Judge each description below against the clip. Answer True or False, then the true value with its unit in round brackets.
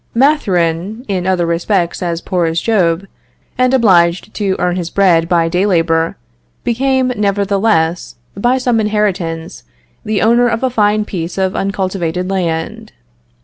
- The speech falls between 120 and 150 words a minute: True (140 wpm)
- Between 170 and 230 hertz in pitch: True (190 Hz)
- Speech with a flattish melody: False (4.1 semitones)